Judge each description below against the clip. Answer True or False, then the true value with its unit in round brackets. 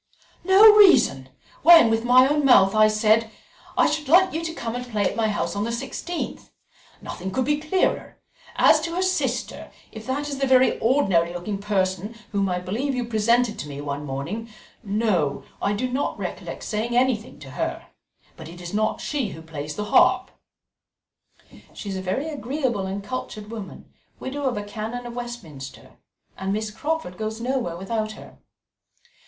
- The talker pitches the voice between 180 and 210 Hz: False (225 Hz)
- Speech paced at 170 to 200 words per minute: True (180 wpm)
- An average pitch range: True (5.0 semitones)